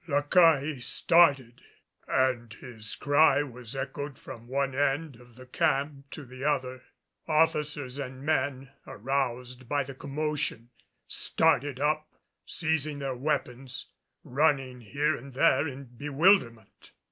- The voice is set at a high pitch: No, low, 135 Hz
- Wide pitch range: No, narrow, 2.6 semitones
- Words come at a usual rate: No, slow, 125 wpm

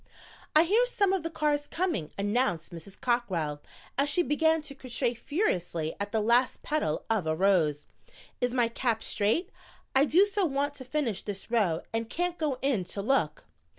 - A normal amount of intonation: No, wide, 7.3 semitones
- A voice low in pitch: No, high, 245 Hz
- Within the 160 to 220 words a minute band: Yes, average, 180 wpm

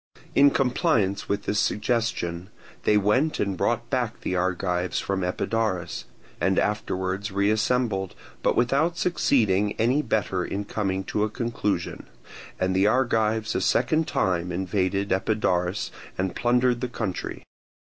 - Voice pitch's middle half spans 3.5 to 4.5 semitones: Yes, average, 4.1 semitones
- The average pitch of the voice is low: Yes, low, 105 Hz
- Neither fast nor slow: No, slow, 130 wpm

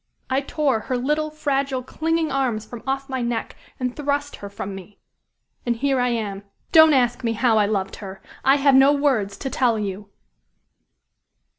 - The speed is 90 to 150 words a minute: No, average, 175 wpm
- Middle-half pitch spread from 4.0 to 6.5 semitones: Yes, average, 4.4 semitones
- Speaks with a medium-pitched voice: No, very high, 255 Hz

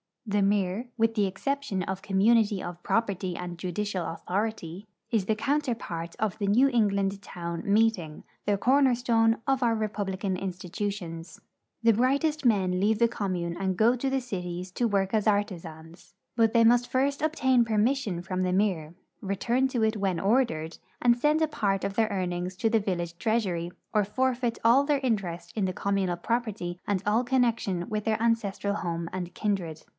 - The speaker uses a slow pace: No, average, 175 wpm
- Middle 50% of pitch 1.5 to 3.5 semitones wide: No, average, 4.2 semitones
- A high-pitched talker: Yes, high, 205 Hz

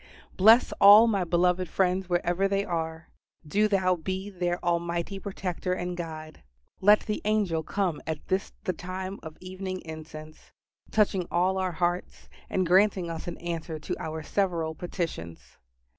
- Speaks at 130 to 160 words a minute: Yes, average, 150 wpm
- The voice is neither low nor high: Yes, medium, 180 Hz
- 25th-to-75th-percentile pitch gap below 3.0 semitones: Yes, narrow, 2.5 semitones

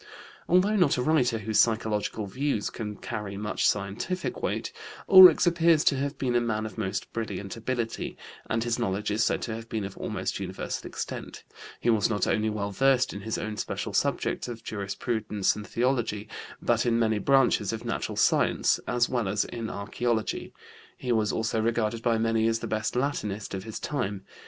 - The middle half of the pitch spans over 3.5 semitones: No, average, 2.7 semitones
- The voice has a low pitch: Yes, low, 115 Hz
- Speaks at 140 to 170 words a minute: No, average, 185 wpm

